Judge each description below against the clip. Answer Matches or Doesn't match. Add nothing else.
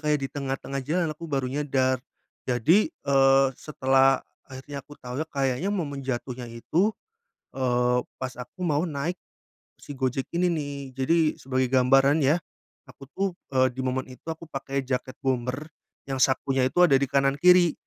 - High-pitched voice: Doesn't match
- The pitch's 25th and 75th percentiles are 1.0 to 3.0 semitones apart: Matches